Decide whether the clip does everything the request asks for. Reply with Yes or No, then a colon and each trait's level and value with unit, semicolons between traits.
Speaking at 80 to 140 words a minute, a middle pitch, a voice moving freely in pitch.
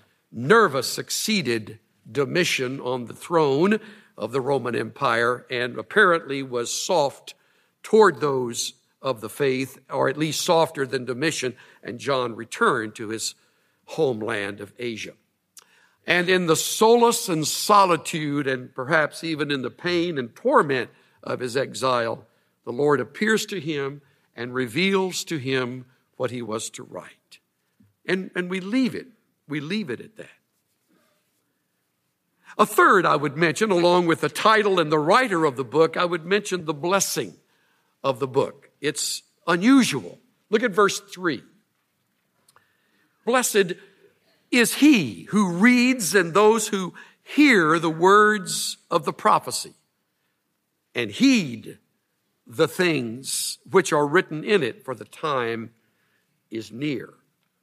Yes: slow, 135 wpm; medium, 160 Hz; wide, 7.5 semitones